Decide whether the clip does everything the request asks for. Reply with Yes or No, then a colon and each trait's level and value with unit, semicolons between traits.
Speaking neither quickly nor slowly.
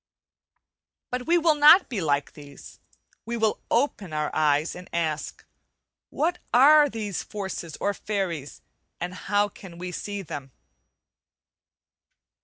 No: slow, 125 wpm